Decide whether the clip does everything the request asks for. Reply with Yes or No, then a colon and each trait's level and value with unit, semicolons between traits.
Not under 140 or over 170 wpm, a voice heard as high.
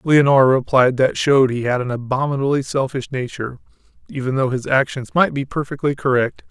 No: average, 165 wpm; low, 135 Hz